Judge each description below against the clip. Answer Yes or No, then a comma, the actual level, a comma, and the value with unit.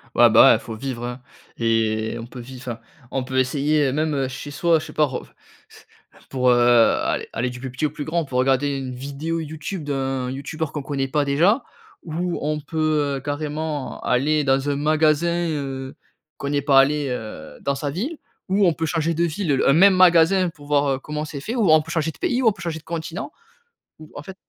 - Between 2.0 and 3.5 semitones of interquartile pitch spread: Yes, average, 3.2 semitones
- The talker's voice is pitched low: No, medium, 145 Hz